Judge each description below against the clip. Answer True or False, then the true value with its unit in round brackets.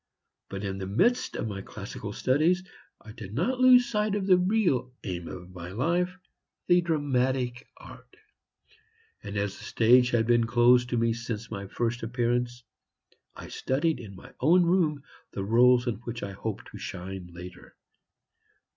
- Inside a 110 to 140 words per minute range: False (165 wpm)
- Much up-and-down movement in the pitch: True (7.8 semitones)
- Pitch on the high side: False (120 Hz)